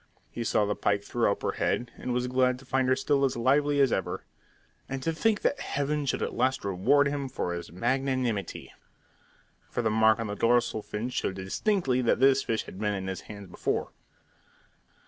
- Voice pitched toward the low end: Yes, low, 125 Hz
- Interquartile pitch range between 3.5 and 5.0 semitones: Yes, average, 4.5 semitones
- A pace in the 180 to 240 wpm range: Yes, average, 200 wpm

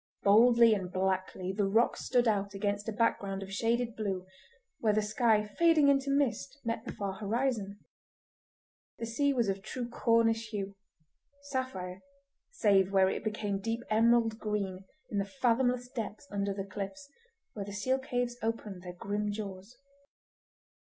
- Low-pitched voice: No, high, 215 Hz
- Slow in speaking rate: No, average, 150 wpm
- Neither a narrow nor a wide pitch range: Yes, average, 3.4 semitones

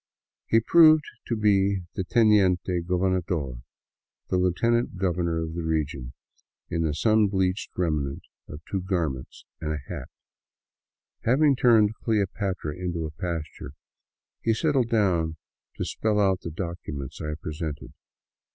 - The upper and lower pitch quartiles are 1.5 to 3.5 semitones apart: No, average, 4.9 semitones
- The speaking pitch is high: No, very low, 90 Hz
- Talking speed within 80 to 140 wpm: Yes, slow, 135 wpm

